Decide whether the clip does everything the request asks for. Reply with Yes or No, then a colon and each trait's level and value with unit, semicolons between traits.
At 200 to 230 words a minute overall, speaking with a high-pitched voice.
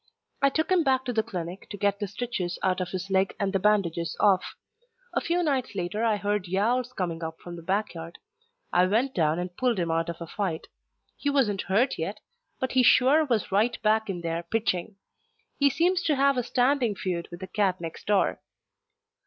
Yes: fast, 205 wpm; high, 205 Hz